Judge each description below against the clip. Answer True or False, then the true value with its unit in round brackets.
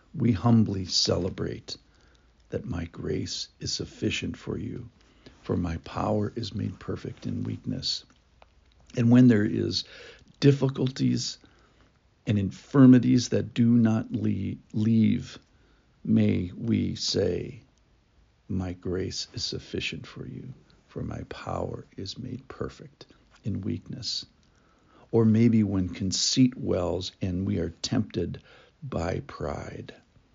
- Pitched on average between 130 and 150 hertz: False (105 Hz)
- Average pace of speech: False (115 wpm)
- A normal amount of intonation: True (4.7 semitones)